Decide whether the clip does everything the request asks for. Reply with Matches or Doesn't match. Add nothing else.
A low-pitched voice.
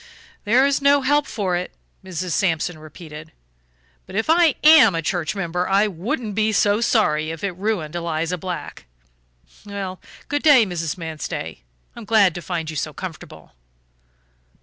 Doesn't match